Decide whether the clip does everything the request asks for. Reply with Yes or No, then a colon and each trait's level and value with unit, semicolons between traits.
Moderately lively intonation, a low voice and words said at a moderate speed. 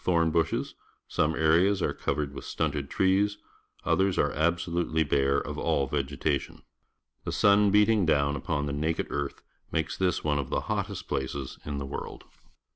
Yes: average, 3.8 semitones; very low, 80 Hz; average, 160 wpm